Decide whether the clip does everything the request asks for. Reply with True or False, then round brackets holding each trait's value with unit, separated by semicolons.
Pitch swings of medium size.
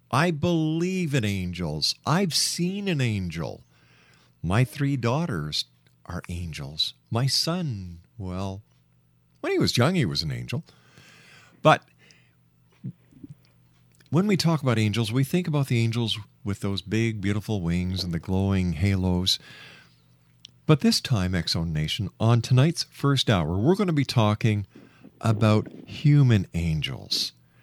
False (8.6 semitones)